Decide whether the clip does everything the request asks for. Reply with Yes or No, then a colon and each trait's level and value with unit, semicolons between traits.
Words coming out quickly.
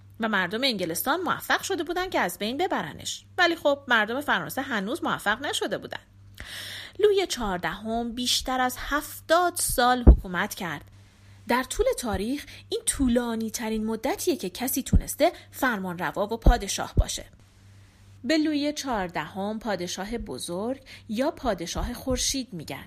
No: average, 130 wpm